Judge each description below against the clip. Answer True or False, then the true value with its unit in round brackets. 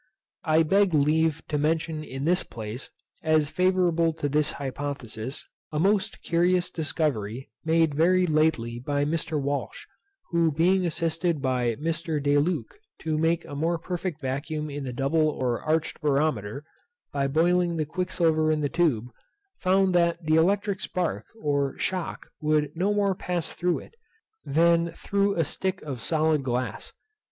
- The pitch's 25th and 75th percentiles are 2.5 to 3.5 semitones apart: True (3.1 semitones)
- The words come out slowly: False (150 wpm)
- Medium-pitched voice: True (155 Hz)